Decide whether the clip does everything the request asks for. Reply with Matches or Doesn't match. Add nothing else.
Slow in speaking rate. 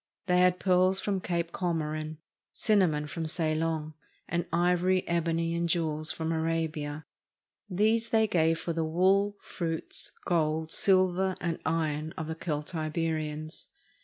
Matches